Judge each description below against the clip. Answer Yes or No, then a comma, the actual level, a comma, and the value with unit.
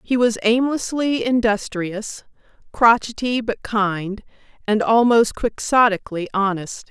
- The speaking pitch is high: Yes, high, 220 Hz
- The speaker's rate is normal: No, slow, 95 wpm